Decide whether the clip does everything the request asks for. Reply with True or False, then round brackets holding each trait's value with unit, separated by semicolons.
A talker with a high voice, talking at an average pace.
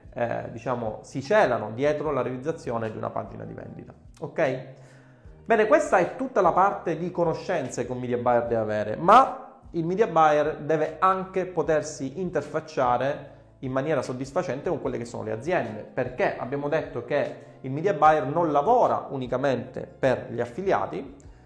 False (145 Hz; 160 wpm)